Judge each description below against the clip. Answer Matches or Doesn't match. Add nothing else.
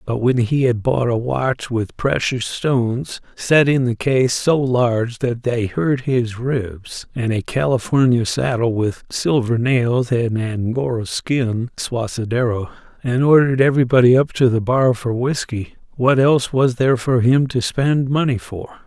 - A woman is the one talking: Doesn't match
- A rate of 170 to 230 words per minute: Doesn't match